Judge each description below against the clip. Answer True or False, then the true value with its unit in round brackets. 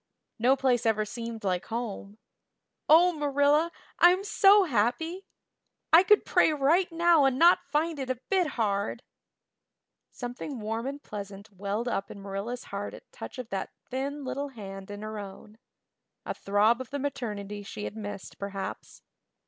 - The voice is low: False (245 Hz)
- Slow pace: False (155 wpm)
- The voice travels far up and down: True (6.3 semitones)